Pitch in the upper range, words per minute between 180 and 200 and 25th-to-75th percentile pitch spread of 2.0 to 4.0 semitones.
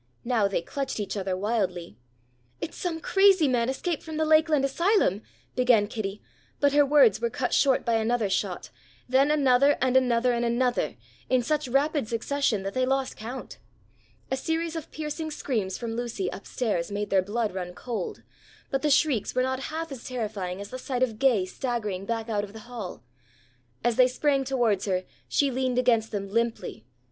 No: high, 245 Hz; average, 185 wpm; average, 4.7 semitones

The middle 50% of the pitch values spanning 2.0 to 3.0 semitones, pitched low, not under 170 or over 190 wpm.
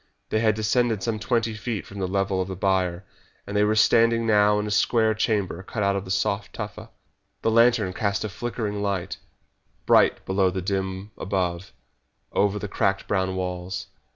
Yes: narrow, 2.5 semitones; low, 100 Hz; average, 180 wpm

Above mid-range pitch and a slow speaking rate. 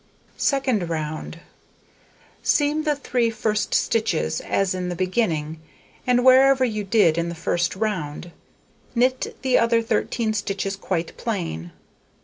Yes: high, 210 Hz; slow, 130 wpm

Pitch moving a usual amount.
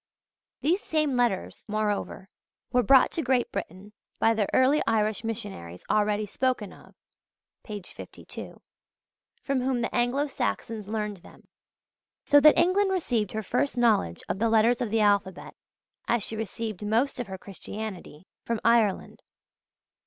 Yes: average, 3.4 semitones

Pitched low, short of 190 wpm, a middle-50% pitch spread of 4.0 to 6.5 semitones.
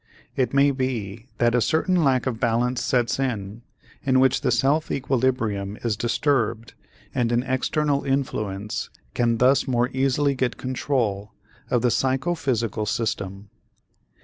No: low, 125 Hz; slow, 135 wpm; average, 2.9 semitones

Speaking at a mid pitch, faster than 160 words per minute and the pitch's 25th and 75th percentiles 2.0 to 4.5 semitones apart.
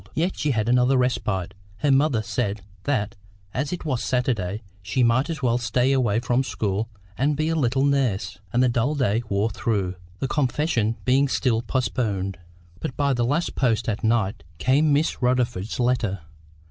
No: low, 125 Hz; average, 170 wpm; average, 3.9 semitones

